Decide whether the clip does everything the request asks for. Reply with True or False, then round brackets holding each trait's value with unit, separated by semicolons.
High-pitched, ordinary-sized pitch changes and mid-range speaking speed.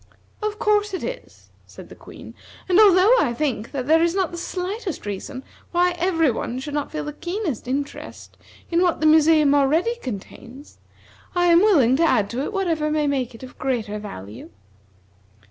False (310 Hz; 5.8 semitones; 180 wpm)